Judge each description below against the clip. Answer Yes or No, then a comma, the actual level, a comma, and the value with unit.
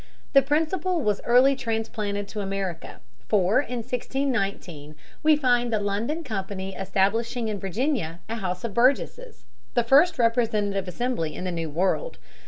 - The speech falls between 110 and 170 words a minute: Yes, average, 145 wpm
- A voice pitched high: Yes, high, 225 Hz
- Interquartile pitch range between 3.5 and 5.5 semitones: Yes, average, 5.1 semitones